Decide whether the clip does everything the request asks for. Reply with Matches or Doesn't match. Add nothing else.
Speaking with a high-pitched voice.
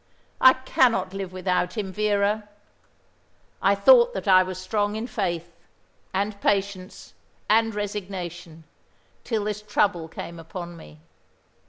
Matches